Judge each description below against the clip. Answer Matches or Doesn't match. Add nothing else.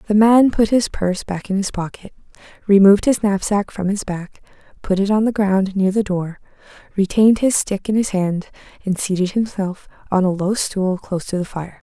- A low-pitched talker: Doesn't match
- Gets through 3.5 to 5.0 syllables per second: Doesn't match